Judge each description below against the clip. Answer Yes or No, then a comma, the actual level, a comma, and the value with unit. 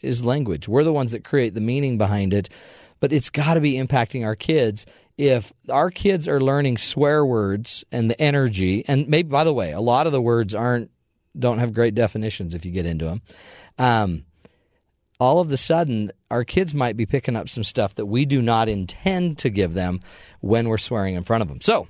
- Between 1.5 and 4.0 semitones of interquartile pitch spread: No, average, 4.7 semitones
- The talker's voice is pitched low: Yes, low, 120 Hz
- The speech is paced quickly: Yes, fast, 215 wpm